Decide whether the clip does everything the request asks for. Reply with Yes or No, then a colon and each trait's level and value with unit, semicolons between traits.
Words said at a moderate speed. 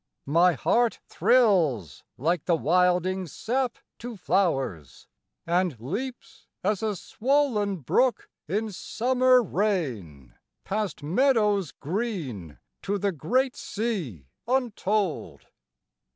No: slow, 95 wpm